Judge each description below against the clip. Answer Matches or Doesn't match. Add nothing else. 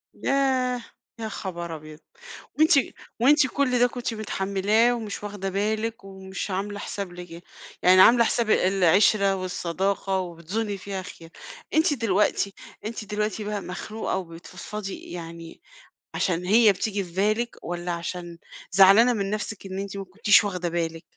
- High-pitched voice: Matches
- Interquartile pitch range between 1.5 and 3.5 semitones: Matches